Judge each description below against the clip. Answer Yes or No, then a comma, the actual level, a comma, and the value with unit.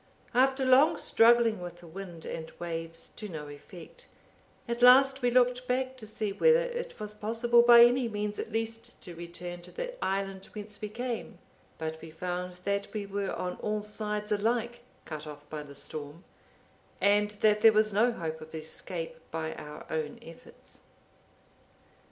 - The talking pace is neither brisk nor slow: Yes, average, 170 wpm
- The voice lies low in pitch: No, high, 210 Hz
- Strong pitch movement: Yes, wide, 5.7 semitones